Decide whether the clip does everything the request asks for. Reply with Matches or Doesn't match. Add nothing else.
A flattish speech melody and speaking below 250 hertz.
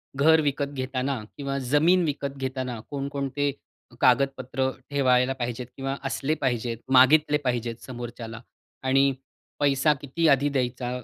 Matches